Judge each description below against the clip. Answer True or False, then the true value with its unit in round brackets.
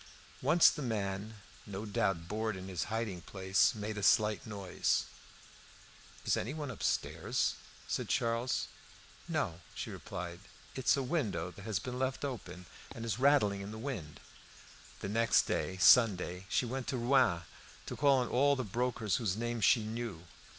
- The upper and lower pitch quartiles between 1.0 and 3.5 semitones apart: False (4.5 semitones)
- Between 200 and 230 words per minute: False (165 wpm)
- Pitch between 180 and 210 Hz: False (110 Hz)